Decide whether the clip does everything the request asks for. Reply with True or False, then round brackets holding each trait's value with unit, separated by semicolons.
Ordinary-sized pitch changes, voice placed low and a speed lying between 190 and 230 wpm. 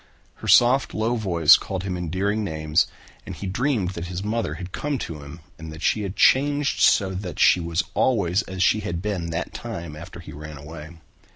True (4.3 semitones; 90 Hz; 200 wpm)